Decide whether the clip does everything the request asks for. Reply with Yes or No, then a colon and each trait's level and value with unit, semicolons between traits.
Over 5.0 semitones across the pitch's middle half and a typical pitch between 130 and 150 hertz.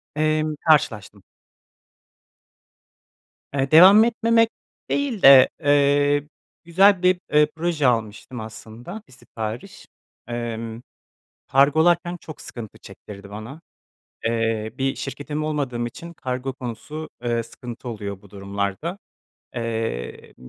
Yes: wide, 5.5 semitones; low, 135 Hz